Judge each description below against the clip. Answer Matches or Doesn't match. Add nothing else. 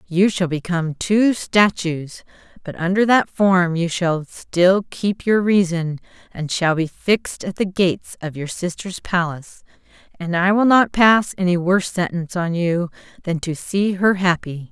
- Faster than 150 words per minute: Matches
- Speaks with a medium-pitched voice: Matches